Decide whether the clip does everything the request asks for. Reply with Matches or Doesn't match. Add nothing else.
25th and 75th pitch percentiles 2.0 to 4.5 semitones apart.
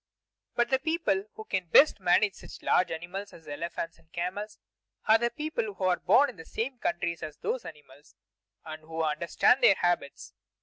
Doesn't match